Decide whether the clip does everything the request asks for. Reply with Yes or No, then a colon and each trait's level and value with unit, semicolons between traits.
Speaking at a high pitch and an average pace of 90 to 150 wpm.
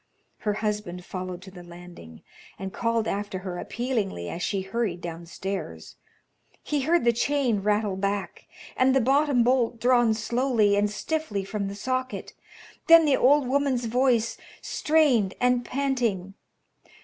Yes: high, 220 Hz; average, 140 wpm